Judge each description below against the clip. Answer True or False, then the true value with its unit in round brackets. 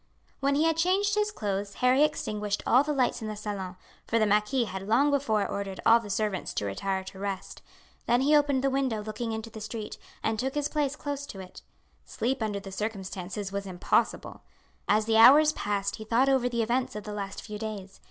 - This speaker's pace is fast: True (210 wpm)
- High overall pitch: True (220 Hz)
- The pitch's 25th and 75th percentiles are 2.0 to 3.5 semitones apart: False (5.0 semitones)